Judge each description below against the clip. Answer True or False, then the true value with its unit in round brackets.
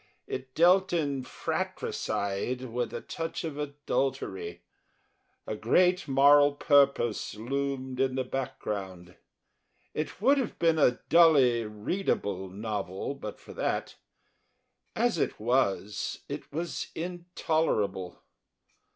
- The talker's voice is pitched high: False (135 Hz)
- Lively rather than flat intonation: True (6.7 semitones)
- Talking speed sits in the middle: False (110 wpm)